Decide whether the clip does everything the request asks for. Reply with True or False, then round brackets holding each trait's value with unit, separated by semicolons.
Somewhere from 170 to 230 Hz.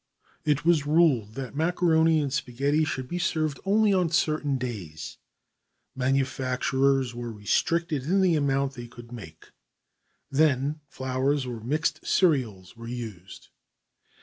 False (135 Hz)